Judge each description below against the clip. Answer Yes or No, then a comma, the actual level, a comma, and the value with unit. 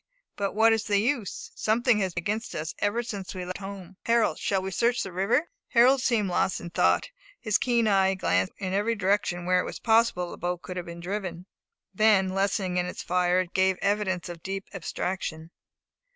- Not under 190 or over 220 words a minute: Yes, fast, 205 wpm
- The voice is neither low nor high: No, high, 195 Hz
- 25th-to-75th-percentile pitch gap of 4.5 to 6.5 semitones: No, average, 3.2 semitones